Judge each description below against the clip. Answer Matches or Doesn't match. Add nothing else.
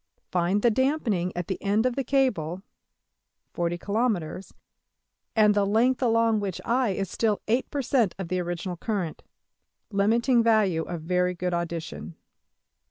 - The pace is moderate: Doesn't match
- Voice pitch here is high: Matches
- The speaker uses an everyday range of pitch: Matches